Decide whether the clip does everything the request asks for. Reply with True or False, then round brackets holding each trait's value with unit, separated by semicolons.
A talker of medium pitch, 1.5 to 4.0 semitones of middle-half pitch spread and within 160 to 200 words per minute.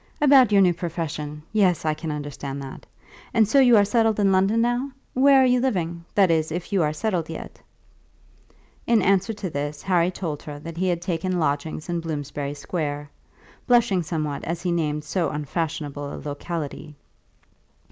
False (170 Hz; 4.7 semitones; 175 wpm)